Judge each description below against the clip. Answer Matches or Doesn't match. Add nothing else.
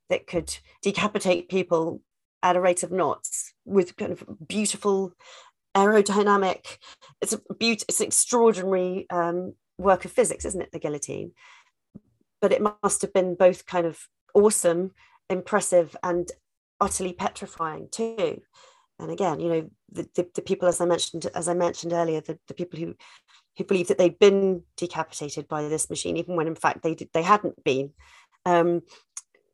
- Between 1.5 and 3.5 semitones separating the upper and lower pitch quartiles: Matches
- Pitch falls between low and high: Matches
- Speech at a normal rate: Matches